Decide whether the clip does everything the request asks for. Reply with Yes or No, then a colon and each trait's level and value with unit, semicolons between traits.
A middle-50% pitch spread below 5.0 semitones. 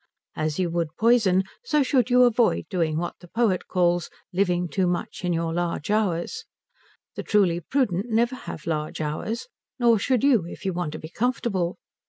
No: wide, 5.4 semitones